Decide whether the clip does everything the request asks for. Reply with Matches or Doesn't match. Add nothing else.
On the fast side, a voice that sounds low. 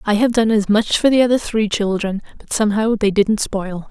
Doesn't match